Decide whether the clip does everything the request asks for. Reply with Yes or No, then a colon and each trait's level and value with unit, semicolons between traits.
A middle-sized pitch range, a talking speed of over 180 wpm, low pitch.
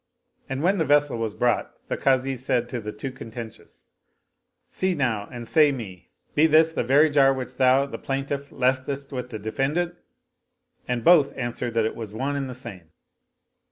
Yes: average, 3.2 semitones; average, 190 wpm; low, 130 Hz